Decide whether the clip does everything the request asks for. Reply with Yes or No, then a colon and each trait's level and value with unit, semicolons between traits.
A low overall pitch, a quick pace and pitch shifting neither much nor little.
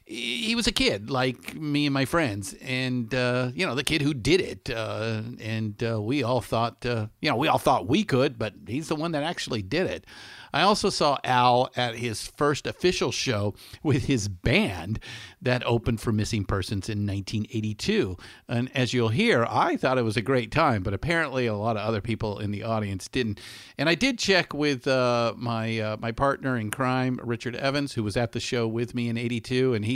Yes: low, 120 Hz; fast, 210 wpm; average, 3.6 semitones